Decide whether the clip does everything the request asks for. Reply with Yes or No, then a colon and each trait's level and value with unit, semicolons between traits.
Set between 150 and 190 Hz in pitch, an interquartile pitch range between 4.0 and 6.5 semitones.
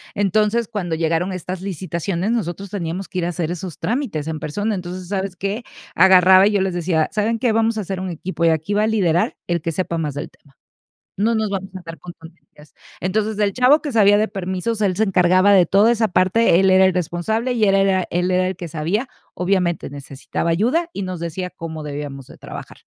No: medium, 185 Hz; average, 3.4 semitones